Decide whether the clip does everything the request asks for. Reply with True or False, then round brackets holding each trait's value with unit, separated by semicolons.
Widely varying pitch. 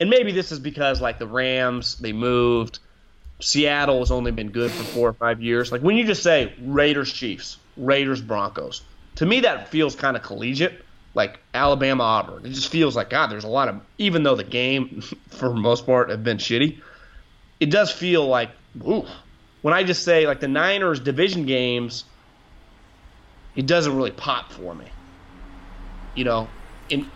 False (4.4 semitones)